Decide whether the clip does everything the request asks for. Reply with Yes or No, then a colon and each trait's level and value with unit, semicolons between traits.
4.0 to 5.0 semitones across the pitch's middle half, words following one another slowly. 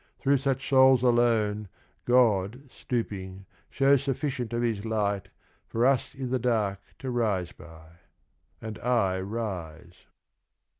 Yes: average, 4.3 semitones; slow, 120 wpm